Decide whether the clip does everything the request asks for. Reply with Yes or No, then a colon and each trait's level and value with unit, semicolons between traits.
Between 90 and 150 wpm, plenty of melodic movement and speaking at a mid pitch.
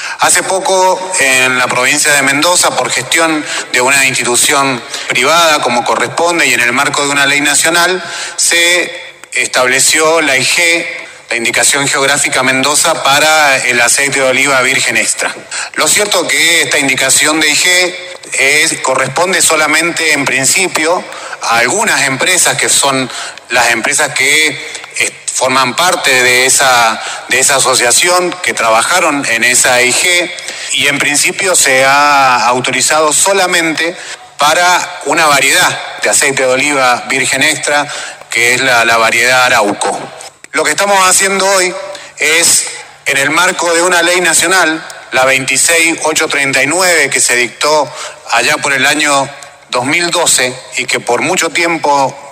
No: average, 140 wpm; average, 4.6 semitones; medium, 145 Hz